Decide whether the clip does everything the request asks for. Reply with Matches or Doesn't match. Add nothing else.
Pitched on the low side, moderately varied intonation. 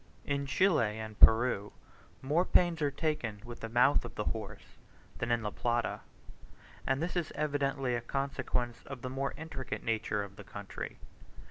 Matches